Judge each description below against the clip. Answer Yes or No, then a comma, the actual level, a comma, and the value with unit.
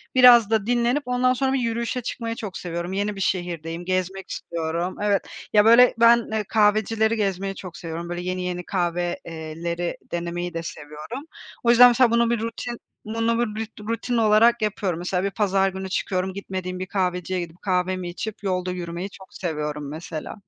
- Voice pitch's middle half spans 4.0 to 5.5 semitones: Yes, average, 4.4 semitones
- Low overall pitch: No, high, 190 Hz